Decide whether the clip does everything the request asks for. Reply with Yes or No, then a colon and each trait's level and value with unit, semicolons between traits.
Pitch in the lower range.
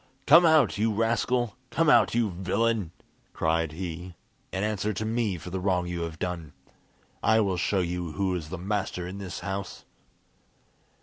Yes: very low, 95 Hz